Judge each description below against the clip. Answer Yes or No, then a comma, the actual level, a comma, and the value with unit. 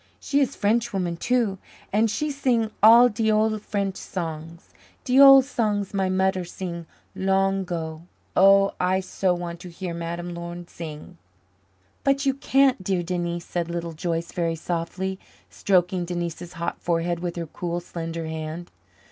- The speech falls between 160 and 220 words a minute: No, average, 150 wpm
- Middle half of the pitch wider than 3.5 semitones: No, average, 3.1 semitones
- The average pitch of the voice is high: No, medium, 180 Hz